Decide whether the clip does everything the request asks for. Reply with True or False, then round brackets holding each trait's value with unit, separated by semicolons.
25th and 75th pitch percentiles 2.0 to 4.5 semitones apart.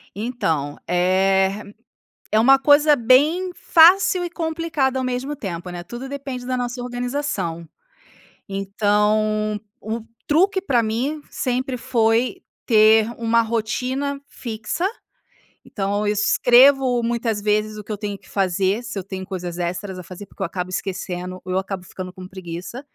False (5.1 semitones)